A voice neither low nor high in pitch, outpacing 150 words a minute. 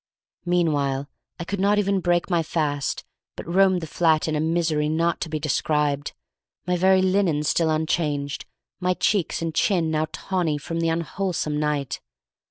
Yes: medium, 165 Hz; average, 165 wpm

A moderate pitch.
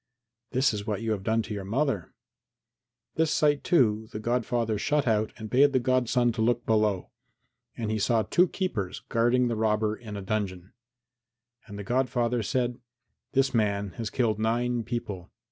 No: low, 115 Hz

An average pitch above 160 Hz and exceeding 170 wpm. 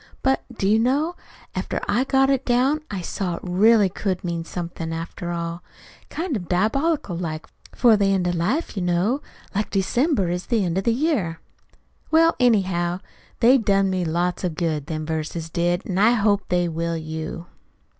Yes: high, 190 Hz; average, 180 wpm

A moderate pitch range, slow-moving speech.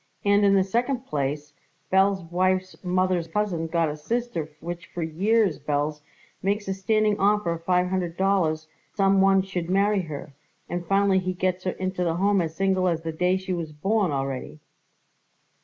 No: average, 3.0 semitones; average, 180 wpm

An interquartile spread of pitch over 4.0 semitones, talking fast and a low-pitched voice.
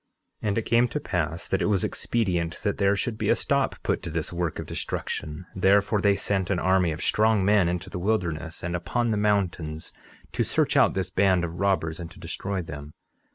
No: average, 3.2 semitones; fast, 215 wpm; very low, 95 Hz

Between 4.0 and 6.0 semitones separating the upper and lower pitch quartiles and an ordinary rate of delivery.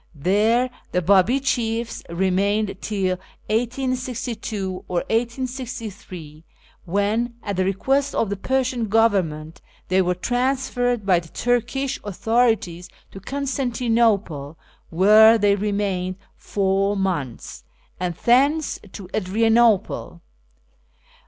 No: average, 4.5 semitones; slow, 100 wpm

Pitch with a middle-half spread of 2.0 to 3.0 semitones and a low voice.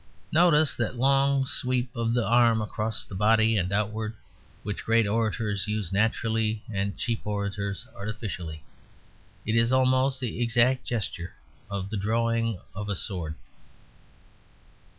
Yes: average, 2.7 semitones; low, 110 Hz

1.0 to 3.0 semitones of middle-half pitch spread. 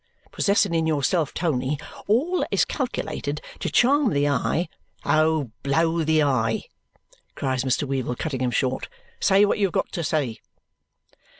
No: average, 4.6 semitones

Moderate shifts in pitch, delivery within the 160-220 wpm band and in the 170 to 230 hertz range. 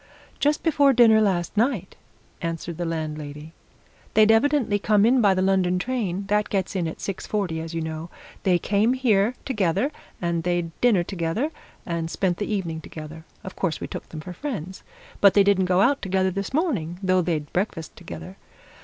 Yes: average, 4.2 semitones; average, 180 wpm; high, 190 Hz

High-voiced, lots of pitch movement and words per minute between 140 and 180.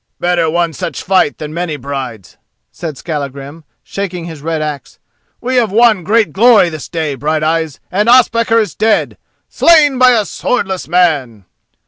No: medium, 170 Hz; wide, 6.1 semitones; average, 145 wpm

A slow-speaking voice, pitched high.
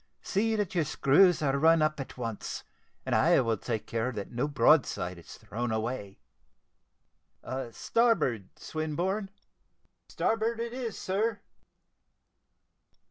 No: slow, 120 wpm; medium, 150 Hz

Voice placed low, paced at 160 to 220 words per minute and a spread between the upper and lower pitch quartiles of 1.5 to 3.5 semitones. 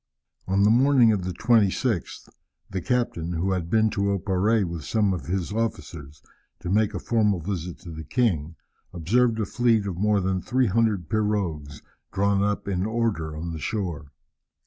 No: low, 100 Hz; average, 170 wpm; average, 4.3 semitones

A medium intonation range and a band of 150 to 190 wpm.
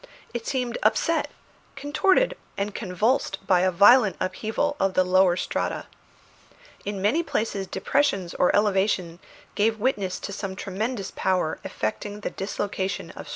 No: average, 3.8 semitones; average, 140 wpm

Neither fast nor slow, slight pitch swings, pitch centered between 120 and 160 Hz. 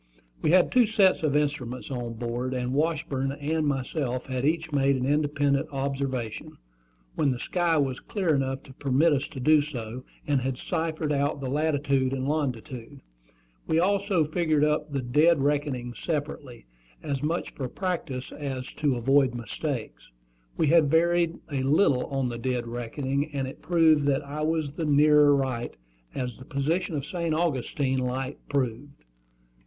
No: average, 165 wpm; average, 3.1 semitones; medium, 140 Hz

